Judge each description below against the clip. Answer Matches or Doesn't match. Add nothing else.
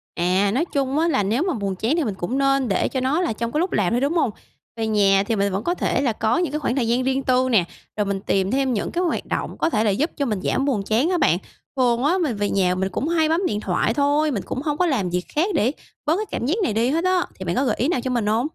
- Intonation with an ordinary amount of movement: Doesn't match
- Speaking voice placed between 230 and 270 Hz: Matches